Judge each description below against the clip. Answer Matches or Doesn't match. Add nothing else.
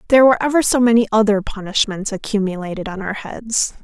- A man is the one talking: Doesn't match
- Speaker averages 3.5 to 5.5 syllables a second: Doesn't match